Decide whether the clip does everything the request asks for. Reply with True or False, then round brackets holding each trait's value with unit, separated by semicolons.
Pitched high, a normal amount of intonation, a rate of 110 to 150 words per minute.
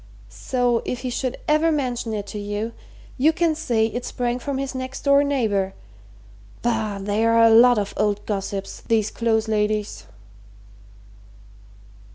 True (230 Hz; 3.5 semitones; 145 wpm)